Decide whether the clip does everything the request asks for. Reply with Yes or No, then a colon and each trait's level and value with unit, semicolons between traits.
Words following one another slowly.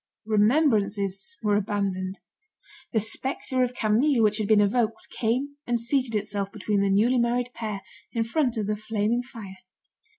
No: average, 155 wpm